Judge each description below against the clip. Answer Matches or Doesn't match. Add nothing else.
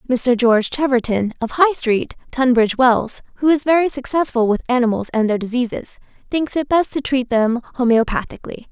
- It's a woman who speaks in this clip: Matches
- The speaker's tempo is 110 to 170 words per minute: Matches